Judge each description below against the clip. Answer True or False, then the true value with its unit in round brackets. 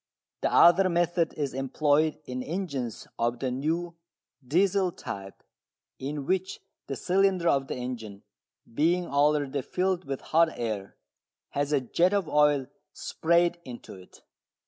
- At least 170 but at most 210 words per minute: False (135 wpm)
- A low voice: False (150 Hz)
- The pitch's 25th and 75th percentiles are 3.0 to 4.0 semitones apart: False (4.9 semitones)